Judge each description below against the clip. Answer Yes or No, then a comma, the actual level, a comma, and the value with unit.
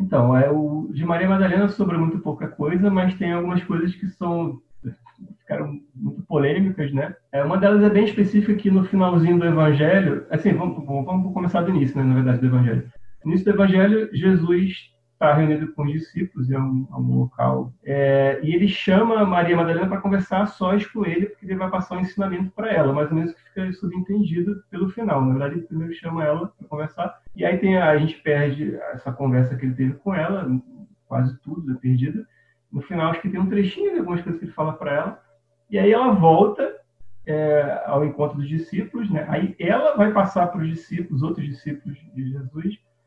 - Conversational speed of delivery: No, fast, 205 wpm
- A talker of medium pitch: Yes, medium, 170 Hz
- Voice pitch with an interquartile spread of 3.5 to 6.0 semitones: Yes, average, 5.1 semitones